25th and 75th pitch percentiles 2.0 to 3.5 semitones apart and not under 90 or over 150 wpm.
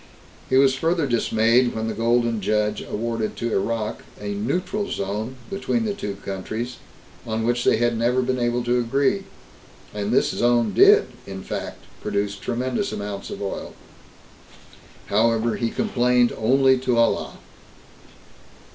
Yes: average, 2.8 semitones; average, 140 wpm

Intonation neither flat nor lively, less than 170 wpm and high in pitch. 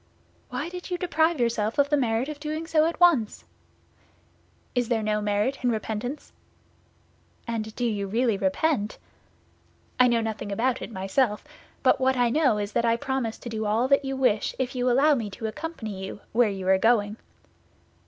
No: average, 4.3 semitones; average, 180 wpm; high, 235 Hz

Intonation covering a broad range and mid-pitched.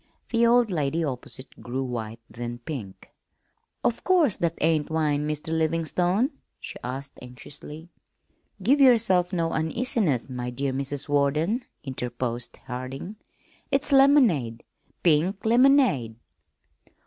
Yes: wide, 8.4 semitones; medium, 155 Hz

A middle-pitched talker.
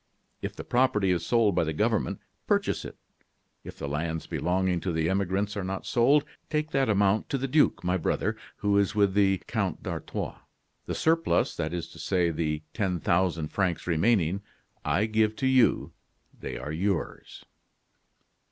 No: very low, 95 Hz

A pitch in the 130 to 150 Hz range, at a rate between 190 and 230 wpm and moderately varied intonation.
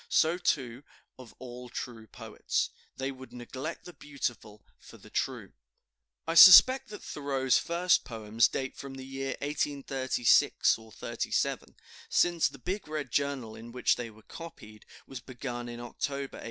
No: low, 135 Hz; average, 150 wpm; average, 3.5 semitones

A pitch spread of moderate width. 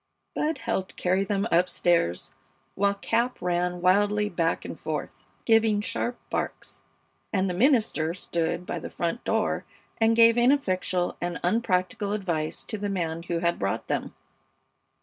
Yes: average, 4.3 semitones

